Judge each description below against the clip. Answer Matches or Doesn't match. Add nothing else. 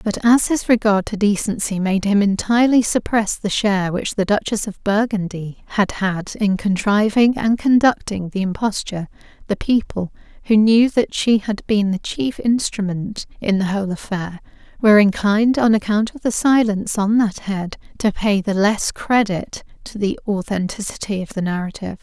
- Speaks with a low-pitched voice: Doesn't match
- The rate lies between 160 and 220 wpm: Matches